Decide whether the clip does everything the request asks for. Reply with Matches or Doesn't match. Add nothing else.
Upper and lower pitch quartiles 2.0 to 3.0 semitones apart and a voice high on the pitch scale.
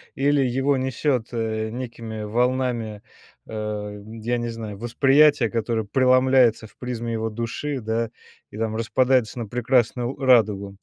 Doesn't match